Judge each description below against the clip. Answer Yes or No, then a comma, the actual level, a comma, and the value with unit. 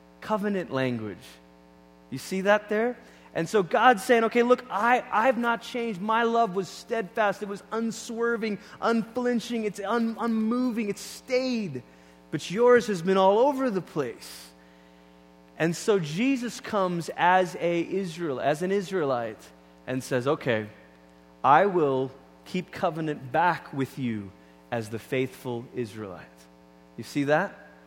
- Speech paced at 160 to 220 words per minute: No, average, 140 wpm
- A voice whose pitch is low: No, medium, 180 Hz